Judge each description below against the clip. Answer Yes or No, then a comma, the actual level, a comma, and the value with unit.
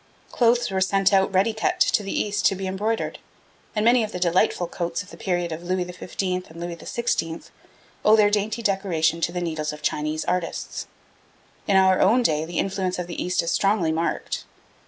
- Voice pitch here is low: No, medium, 185 Hz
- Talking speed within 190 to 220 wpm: Yes, average, 200 wpm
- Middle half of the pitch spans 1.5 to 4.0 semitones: Yes, average, 3.1 semitones